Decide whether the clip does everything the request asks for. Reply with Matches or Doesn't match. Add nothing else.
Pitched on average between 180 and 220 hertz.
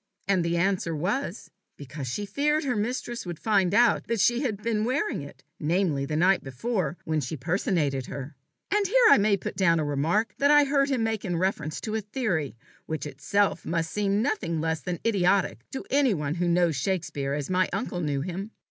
Matches